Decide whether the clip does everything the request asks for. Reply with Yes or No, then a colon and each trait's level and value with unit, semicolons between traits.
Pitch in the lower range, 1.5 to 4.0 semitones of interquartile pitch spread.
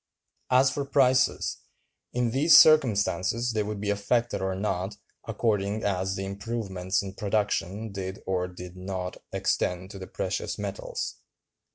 Yes: low, 100 Hz; average, 3.6 semitones